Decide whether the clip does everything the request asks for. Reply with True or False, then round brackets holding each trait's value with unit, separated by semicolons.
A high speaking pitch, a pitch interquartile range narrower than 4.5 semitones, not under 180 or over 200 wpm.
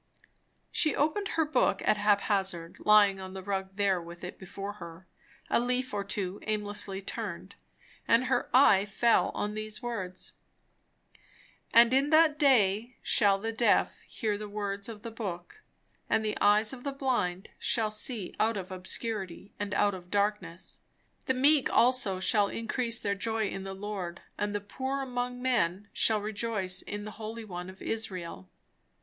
False (210 Hz; 3.3 semitones; 165 wpm)